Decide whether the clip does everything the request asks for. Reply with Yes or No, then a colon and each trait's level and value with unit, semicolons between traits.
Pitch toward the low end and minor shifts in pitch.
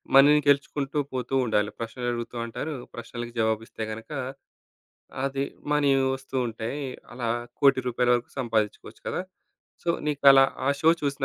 No: low, 125 Hz; average, 3.3 semitones